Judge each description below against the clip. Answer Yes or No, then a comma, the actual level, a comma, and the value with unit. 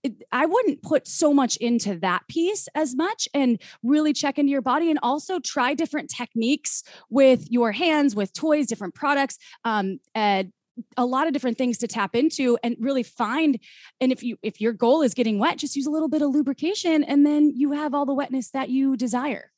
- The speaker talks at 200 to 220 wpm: Yes, fast, 205 wpm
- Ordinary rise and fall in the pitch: Yes, average, 3.9 semitones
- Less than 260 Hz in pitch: No, very high, 270 Hz